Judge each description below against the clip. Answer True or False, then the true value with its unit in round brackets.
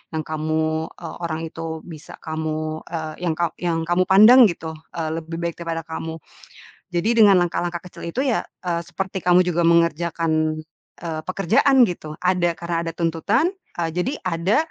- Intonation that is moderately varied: False (1.9 semitones)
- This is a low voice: False (170 Hz)